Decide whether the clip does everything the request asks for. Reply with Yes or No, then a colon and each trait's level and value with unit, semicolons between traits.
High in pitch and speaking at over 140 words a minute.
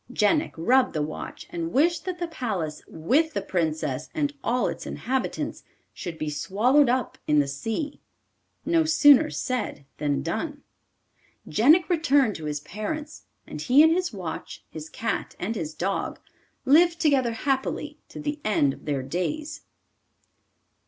Yes: high, 245 Hz; average, 150 wpm